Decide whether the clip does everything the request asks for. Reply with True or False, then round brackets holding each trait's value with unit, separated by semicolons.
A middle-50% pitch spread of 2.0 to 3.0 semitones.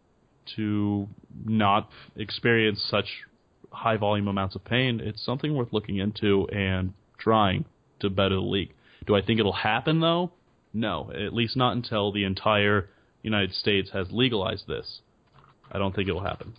True (2.5 semitones)